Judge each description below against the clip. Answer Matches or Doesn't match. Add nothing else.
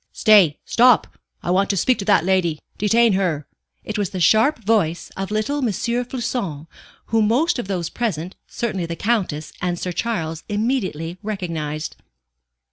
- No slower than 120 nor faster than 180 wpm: Matches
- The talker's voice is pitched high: Matches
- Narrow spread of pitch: Doesn't match